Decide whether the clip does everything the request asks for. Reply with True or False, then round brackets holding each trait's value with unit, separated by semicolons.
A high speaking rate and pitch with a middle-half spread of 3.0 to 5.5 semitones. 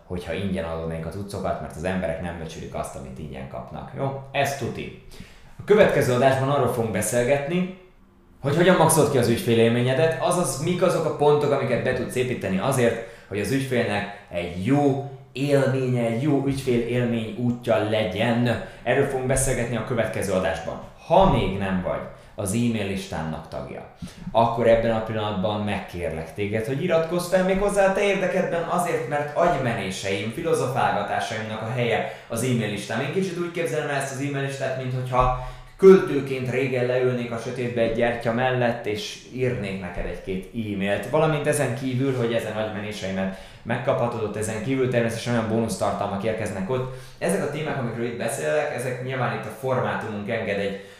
True (160 wpm; 4.9 semitones)